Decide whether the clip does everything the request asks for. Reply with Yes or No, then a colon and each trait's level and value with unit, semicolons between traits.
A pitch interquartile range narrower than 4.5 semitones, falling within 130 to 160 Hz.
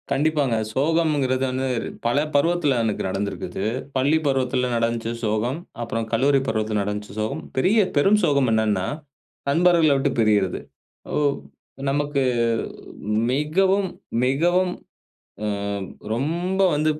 No: wide, 5.6 semitones; low, 135 Hz